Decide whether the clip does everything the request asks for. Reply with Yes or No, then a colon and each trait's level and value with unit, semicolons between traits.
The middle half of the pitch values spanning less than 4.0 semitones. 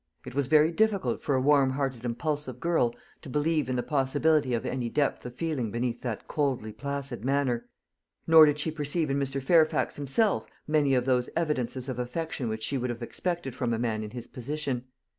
Yes: average, 3.6 semitones